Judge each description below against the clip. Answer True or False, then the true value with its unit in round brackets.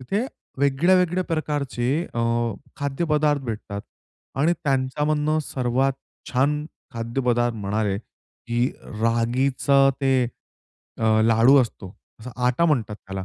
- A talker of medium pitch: False (130 Hz)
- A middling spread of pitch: True (4.1 semitones)